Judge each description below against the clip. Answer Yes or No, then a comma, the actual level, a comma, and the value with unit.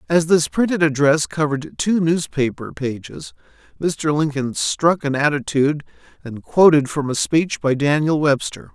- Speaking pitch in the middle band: Yes, medium, 150 Hz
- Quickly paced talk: No, average, 145 wpm